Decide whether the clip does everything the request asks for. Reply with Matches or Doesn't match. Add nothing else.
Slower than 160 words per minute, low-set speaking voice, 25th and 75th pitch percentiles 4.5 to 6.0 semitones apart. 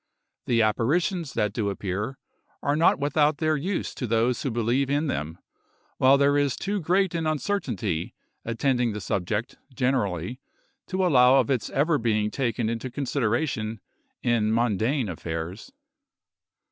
Matches